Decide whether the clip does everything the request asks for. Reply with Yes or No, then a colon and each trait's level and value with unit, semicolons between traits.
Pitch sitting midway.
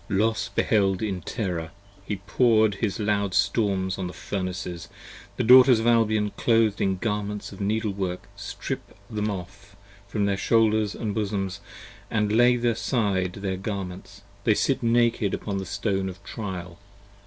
No: low, 100 Hz